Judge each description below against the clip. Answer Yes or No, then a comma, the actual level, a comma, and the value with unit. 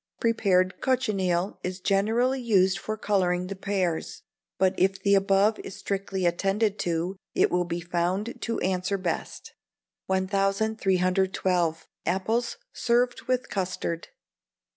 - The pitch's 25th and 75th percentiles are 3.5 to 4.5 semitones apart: No, narrow, 2.5 semitones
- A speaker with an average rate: No, slow, 120 wpm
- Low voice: No, high, 195 Hz